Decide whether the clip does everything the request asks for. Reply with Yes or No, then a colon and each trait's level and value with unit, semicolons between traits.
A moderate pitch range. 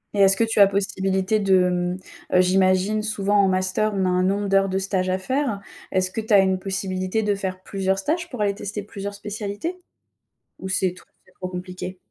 No: narrow, 1.7 semitones